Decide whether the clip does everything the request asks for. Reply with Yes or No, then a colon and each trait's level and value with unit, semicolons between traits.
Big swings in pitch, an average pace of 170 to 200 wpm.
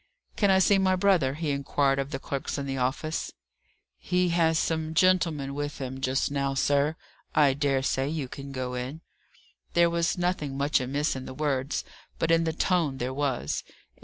No: average, 3.5 semitones; average, 185 wpm